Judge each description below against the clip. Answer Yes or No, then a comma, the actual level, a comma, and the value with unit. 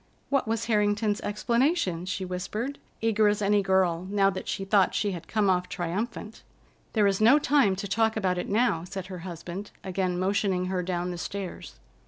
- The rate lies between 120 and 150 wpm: No, average, 185 wpm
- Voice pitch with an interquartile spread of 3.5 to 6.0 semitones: No, average, 2.8 semitones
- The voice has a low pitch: No, high, 195 Hz